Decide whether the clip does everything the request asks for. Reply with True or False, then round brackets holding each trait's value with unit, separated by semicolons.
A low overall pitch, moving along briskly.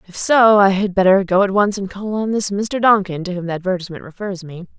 False (195 Hz; 250 wpm)